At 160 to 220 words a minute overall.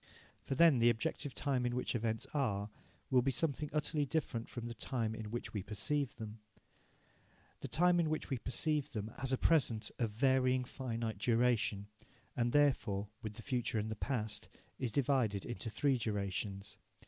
Yes: average, 170 wpm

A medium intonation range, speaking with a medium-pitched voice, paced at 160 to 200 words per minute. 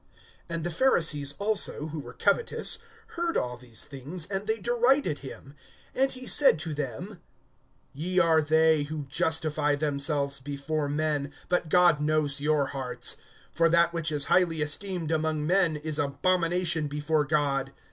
No: average, 3.3 semitones; medium, 155 Hz; average, 150 wpm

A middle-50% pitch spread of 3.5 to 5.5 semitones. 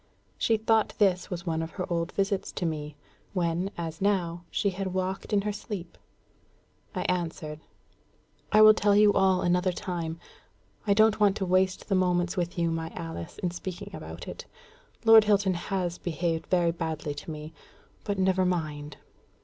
No: average, 2.9 semitones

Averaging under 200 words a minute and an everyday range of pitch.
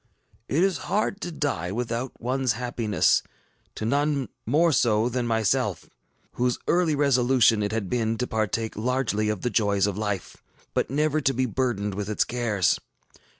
Yes: average, 160 wpm; average, 3.9 semitones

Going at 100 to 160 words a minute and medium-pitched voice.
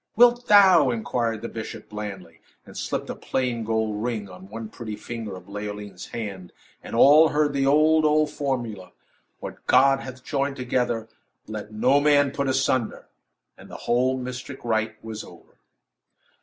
No: average, 155 wpm; low, 120 Hz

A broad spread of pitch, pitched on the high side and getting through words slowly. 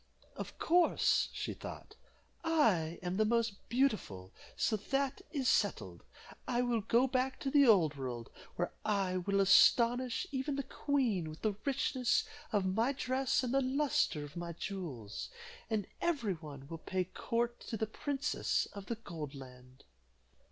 No: wide, 7.3 semitones; high, 220 Hz; average, 155 wpm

